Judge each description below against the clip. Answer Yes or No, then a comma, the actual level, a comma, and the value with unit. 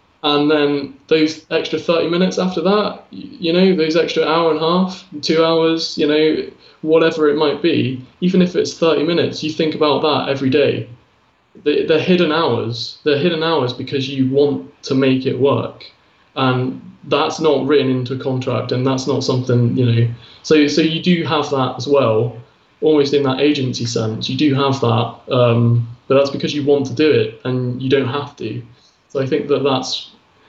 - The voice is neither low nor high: Yes, medium, 145 Hz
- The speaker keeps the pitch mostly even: No, average, 3.5 semitones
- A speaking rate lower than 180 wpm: No, average, 190 wpm